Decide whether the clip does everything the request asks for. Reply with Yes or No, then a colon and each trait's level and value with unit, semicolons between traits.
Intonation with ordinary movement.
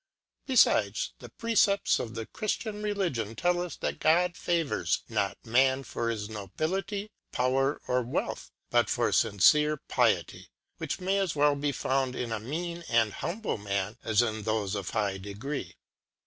No: wide, 8.1 semitones